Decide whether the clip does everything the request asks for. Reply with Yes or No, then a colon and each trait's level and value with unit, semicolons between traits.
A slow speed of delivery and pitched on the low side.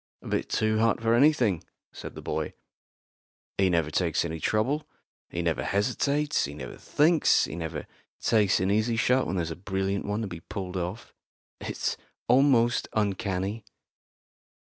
No: average, 155 wpm; low, 100 Hz